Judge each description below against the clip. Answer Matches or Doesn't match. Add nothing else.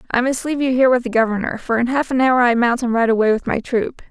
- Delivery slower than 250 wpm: Doesn't match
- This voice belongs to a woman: Matches